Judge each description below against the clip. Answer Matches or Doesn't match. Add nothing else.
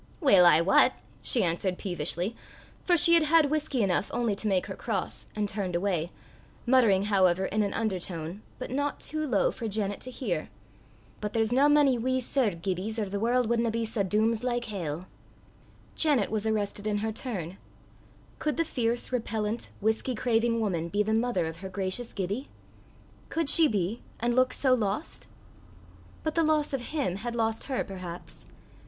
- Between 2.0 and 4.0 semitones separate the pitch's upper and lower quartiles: Doesn't match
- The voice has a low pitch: Doesn't match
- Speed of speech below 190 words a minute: Matches